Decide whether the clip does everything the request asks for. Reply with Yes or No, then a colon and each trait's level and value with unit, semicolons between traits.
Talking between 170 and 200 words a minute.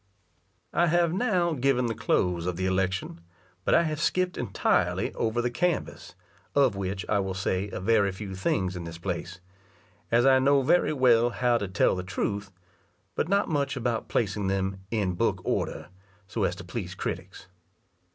Yes: average, 175 wpm